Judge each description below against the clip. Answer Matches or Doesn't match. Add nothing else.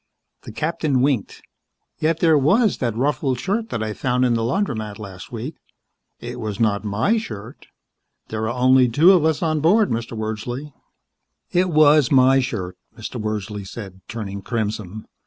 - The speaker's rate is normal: Matches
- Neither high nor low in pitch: Doesn't match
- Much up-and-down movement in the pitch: Matches